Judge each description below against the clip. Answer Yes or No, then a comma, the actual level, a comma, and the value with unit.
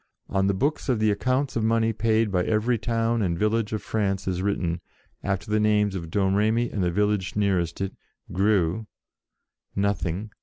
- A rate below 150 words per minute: No, average, 175 wpm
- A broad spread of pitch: No, narrow, 2.6 semitones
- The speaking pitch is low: Yes, low, 105 Hz